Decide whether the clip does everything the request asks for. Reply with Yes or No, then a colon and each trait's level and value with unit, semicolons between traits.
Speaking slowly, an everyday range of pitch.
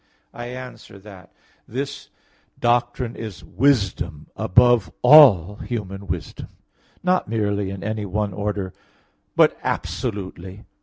Yes: slow, 105 wpm; average, 4.0 semitones